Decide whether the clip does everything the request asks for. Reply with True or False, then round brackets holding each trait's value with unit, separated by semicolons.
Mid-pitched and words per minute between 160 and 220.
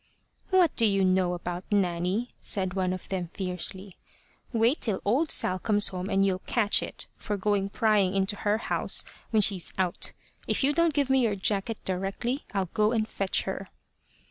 False (200 Hz; 180 wpm)